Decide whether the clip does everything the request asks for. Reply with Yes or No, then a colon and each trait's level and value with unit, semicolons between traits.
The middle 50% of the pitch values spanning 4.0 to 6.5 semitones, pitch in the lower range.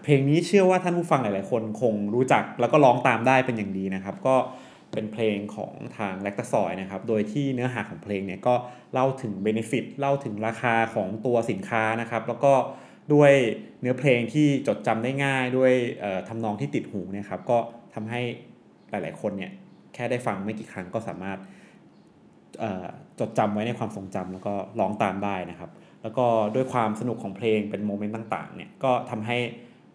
No: average, 3.6 semitones; low, 115 Hz